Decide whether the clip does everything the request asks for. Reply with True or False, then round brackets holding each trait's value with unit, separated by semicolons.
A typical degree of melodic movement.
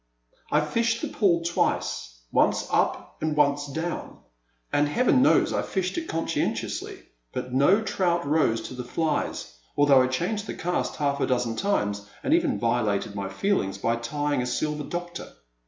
False (6.2 semitones)